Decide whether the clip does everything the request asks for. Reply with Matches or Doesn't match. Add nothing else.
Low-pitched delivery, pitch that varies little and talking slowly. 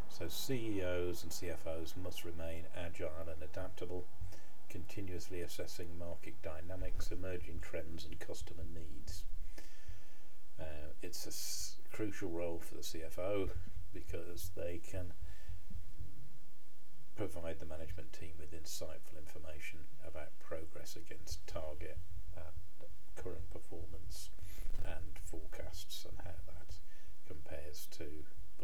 Matches